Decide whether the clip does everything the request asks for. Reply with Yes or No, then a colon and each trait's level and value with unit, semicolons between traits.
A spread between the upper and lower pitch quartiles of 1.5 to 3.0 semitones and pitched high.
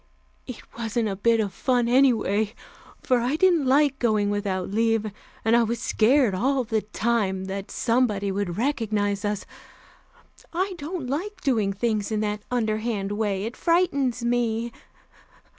No: average, 3.6 semitones; high, 225 Hz